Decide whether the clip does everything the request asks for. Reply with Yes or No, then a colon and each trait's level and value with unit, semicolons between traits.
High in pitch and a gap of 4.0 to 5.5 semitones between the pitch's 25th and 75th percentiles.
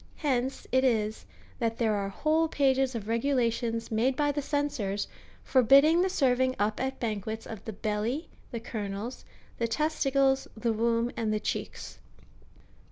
No: high, 240 Hz; average, 3.6 semitones